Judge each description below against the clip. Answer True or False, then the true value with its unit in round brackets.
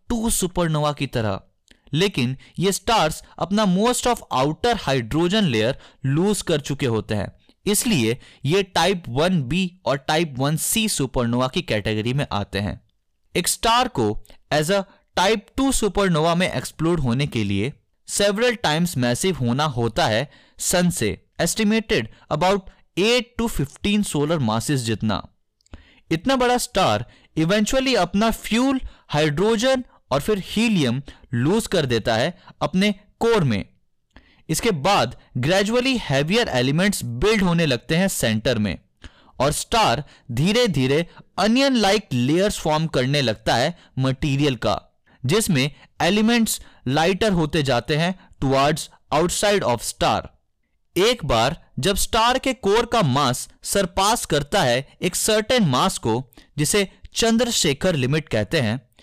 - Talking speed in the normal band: True (135 wpm)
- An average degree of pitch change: False (8.1 semitones)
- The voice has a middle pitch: True (160 Hz)